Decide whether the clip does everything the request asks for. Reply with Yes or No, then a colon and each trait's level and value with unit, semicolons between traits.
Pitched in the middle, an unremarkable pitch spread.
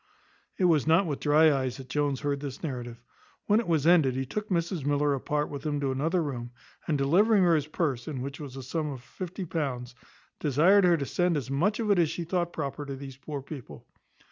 Yes: medium, 150 Hz; average, 3.9 semitones